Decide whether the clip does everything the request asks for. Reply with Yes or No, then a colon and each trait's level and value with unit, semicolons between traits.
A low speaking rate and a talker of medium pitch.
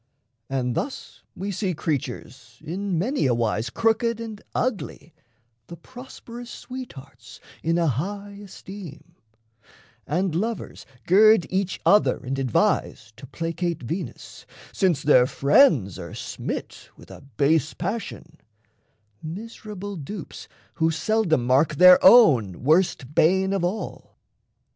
Yes: slow, 120 wpm; medium, 170 Hz